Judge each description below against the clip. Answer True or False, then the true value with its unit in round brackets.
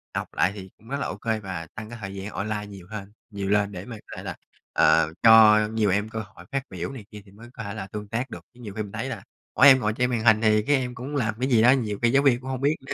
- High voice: False (110 Hz)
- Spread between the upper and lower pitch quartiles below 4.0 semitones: True (3.5 semitones)